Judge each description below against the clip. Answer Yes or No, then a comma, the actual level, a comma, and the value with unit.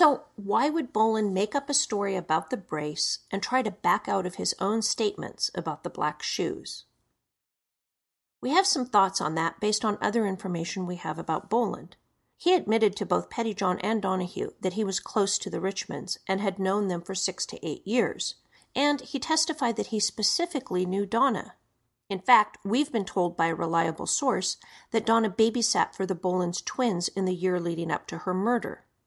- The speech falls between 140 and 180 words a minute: No, average, 195 wpm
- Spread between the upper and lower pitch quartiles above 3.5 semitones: Yes, average, 4.0 semitones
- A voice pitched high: Yes, high, 200 Hz